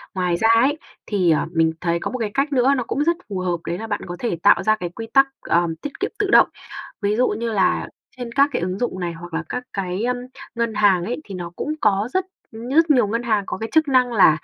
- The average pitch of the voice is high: Yes, high, 215 Hz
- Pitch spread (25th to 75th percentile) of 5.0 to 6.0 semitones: Yes, wide, 5.6 semitones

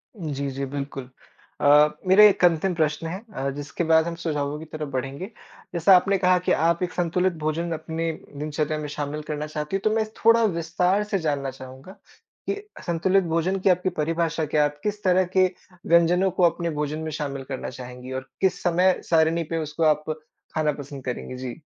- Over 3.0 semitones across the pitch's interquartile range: Yes, average, 3.6 semitones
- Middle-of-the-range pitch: Yes, medium, 160 Hz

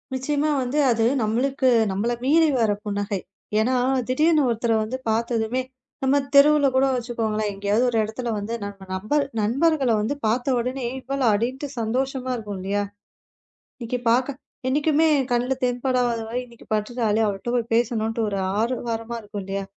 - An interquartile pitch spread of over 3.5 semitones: No, average, 3.2 semitones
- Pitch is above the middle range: Yes, high, 240 Hz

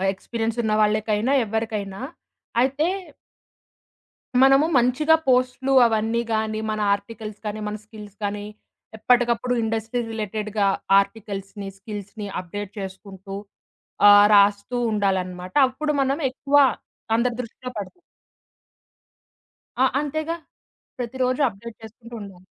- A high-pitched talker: Yes, high, 220 Hz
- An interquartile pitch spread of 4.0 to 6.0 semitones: No, average, 3.5 semitones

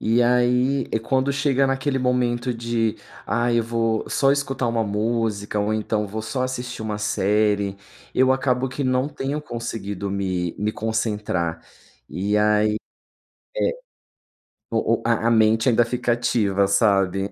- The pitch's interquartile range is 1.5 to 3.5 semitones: Yes, average, 3.2 semitones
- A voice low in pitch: Yes, low, 115 Hz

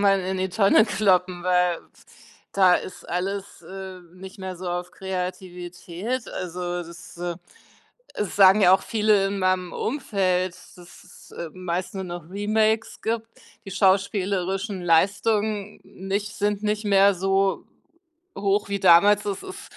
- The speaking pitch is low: No, high, 190 Hz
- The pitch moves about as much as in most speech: No, narrow, 2.1 semitones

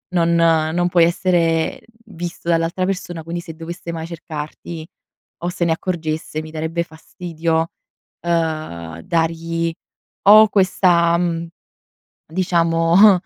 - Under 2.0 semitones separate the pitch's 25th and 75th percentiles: Yes, narrow, 1.3 semitones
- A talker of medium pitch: Yes, medium, 165 Hz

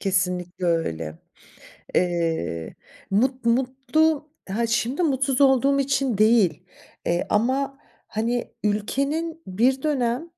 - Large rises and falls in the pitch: Yes, wide, 6.4 semitones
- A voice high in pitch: Yes, high, 240 Hz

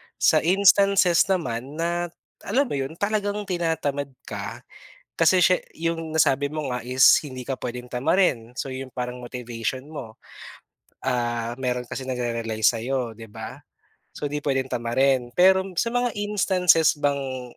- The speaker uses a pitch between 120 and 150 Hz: Yes, low, 135 Hz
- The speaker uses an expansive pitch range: Yes, wide, 5.9 semitones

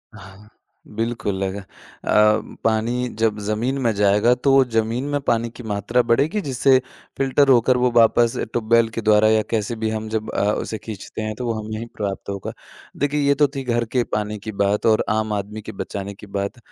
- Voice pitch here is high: No, low, 110 Hz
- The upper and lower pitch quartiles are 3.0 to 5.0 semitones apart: No, narrow, 2.6 semitones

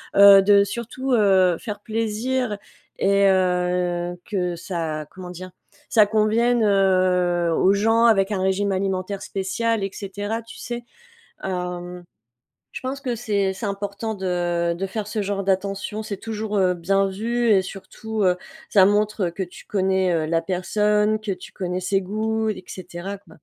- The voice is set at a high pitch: Yes, high, 195 Hz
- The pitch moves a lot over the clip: No, average, 2.7 semitones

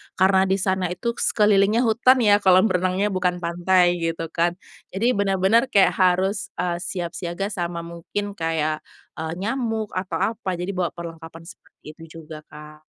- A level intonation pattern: No, average, 3.0 semitones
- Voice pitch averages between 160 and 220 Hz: Yes, medium, 185 Hz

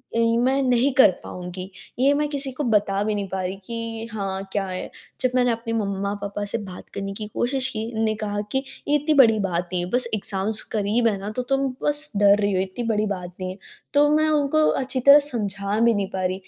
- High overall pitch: Yes, high, 215 Hz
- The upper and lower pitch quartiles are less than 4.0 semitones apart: No, average, 4.4 semitones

